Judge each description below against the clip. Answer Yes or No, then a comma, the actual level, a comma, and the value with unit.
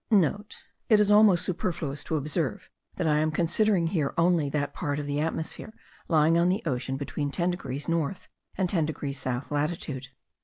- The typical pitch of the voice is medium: Yes, medium, 160 Hz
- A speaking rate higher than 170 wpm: Yes, average, 180 wpm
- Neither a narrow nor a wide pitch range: Yes, average, 3.5 semitones